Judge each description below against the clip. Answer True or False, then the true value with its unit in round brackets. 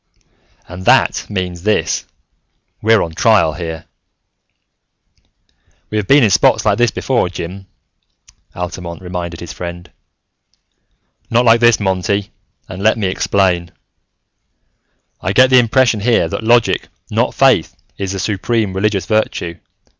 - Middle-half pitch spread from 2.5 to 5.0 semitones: True (4.0 semitones)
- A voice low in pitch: True (95 Hz)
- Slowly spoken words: True (130 wpm)